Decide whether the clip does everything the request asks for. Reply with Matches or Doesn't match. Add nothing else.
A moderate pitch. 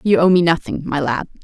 Matches